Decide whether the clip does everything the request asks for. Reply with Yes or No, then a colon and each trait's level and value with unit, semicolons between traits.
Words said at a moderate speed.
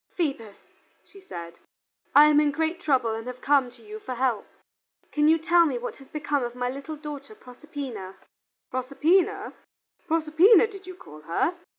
Yes: average, 170 wpm